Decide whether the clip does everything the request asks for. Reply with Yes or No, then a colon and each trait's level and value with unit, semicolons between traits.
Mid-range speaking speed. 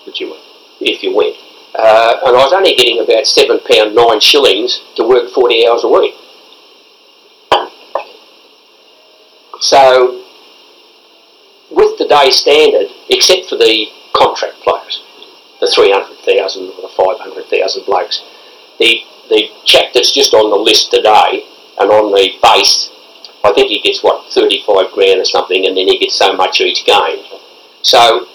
Yes: average, 150 wpm